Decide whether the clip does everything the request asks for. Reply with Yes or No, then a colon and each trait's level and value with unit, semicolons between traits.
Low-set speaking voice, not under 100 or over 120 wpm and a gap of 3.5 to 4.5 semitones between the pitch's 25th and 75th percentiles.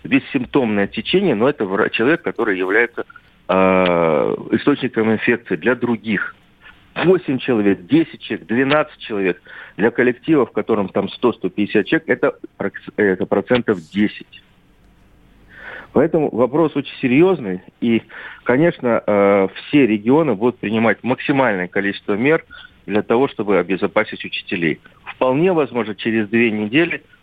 No: low, 110 Hz; average, 115 wpm; average, 5.0 semitones